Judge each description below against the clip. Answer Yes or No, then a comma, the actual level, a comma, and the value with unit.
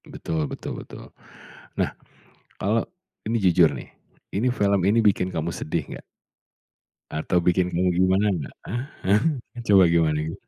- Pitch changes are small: No, average, 3.2 semitones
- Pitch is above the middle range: No, very low, 90 Hz